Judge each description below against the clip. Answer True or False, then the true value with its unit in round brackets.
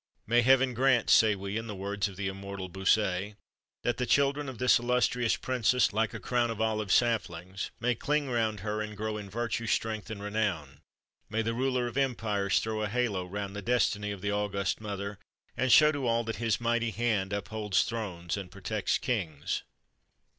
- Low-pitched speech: True (110 Hz)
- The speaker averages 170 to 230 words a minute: True (190 wpm)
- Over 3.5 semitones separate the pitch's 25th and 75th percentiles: False (3.0 semitones)